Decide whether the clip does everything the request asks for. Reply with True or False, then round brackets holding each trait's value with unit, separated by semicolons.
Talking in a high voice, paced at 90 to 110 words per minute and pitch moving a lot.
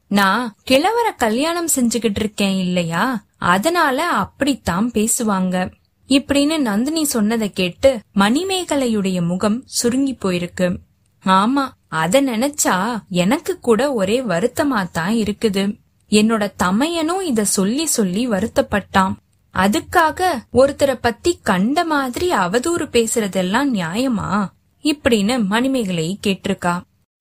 True (230 Hz; 95 wpm; 5.9 semitones)